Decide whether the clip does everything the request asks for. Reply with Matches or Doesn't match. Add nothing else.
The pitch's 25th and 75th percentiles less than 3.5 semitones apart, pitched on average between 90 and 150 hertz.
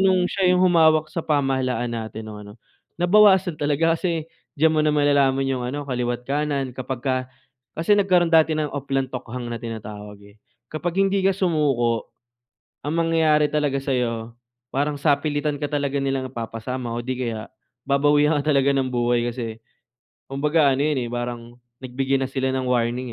Doesn't match